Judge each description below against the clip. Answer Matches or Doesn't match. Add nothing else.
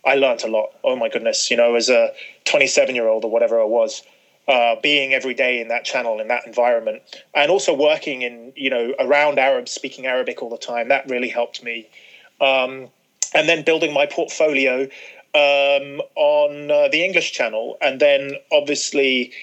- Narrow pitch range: Doesn't match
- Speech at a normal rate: Matches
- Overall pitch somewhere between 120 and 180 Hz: Matches